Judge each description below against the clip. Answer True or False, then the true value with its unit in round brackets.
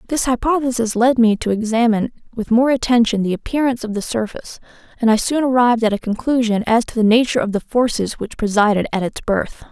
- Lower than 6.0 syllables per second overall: False (6.3 syllables/s)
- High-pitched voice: True (230 Hz)